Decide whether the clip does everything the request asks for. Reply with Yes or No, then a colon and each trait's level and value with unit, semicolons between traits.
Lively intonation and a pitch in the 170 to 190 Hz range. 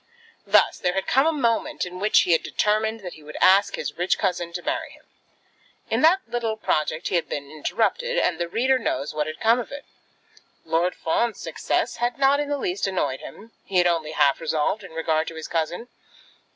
Yes: wide, 6.3 semitones; medium, 185 Hz